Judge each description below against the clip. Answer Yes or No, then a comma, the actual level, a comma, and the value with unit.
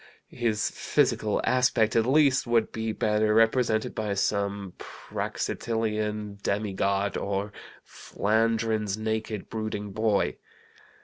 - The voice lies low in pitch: Yes, low, 110 Hz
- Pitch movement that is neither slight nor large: No, narrow, 1.6 semitones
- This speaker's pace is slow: Yes, slow, 100 wpm